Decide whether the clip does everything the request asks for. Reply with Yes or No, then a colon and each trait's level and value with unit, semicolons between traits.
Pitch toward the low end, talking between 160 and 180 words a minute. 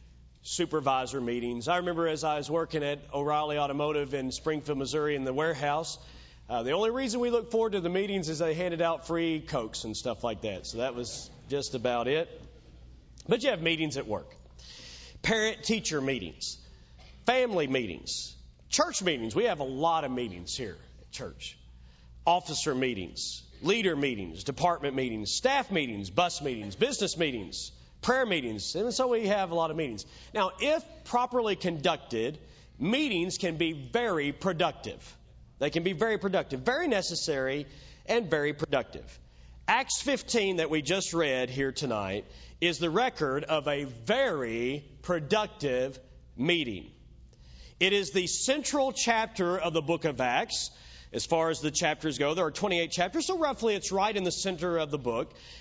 No: medium, 150 Hz; average, 165 wpm